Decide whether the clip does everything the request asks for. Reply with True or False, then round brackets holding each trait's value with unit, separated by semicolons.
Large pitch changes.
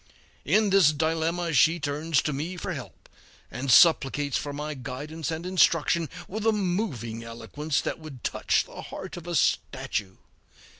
False (3.7 semitones)